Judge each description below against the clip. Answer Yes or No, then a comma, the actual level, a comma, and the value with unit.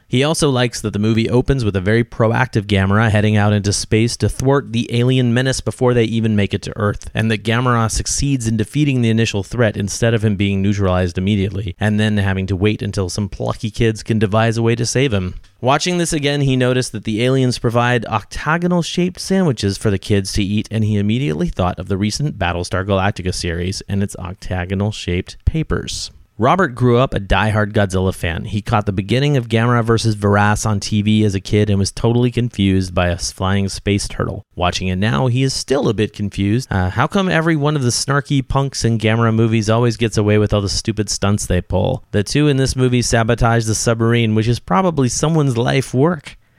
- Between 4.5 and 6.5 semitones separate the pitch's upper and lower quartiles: No, average, 3.5 semitones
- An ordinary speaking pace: No, fast, 215 wpm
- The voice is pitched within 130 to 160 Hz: No, low, 110 Hz